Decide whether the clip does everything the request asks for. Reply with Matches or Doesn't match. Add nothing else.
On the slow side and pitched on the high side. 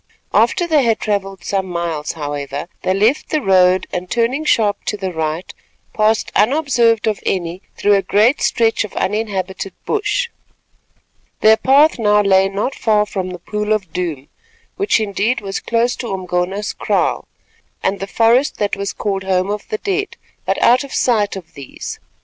Doesn't match